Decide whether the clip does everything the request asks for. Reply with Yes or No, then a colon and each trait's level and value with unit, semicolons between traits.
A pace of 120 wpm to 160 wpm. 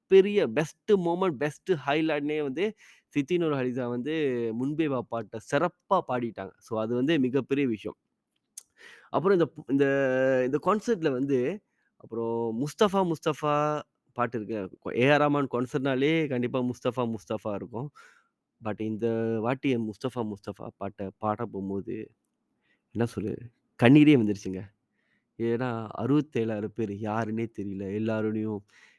No: average, 110 wpm